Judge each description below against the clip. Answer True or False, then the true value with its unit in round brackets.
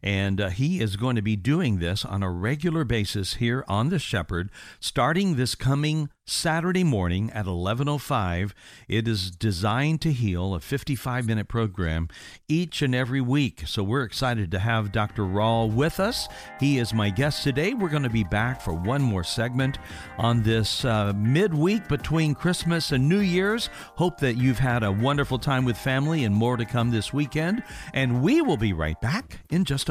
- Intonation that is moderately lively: False (5.8 semitones)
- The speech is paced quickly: False (185 wpm)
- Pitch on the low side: True (125 Hz)